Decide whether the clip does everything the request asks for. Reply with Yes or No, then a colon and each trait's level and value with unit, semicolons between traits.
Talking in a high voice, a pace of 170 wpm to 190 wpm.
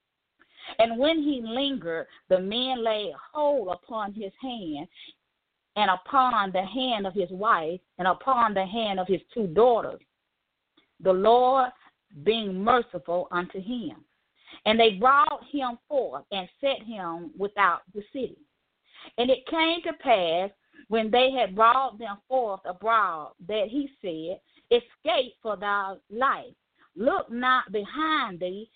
No: high, 230 Hz; average, 140 wpm